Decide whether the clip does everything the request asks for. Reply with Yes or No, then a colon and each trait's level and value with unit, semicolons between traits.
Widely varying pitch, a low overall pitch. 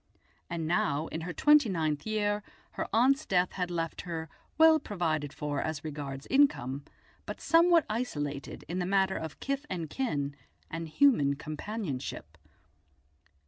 No: wide, 7.0 semitones; medium, 170 Hz